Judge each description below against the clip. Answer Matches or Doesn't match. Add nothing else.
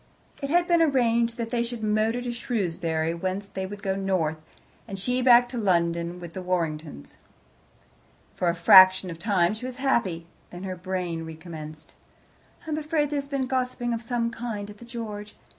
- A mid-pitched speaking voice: Doesn't match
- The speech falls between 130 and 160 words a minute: Doesn't match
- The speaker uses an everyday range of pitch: Doesn't match